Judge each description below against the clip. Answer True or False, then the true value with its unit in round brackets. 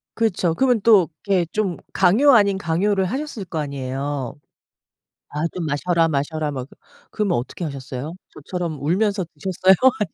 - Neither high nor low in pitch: True (175 Hz)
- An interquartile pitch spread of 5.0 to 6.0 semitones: True (5.4 semitones)